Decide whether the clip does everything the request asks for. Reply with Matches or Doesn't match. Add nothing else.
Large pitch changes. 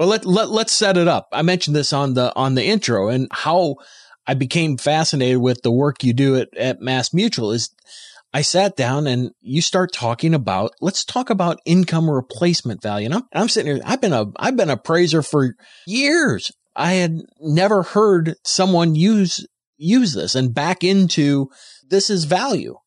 Matches